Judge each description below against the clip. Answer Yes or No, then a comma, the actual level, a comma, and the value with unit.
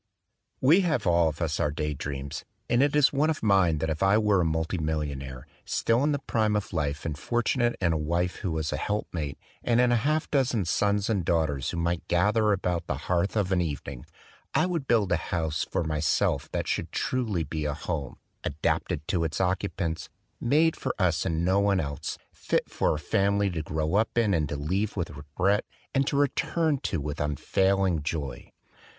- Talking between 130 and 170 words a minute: No, fast, 205 wpm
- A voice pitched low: Yes, very low, 90 Hz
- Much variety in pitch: Yes, wide, 5.7 semitones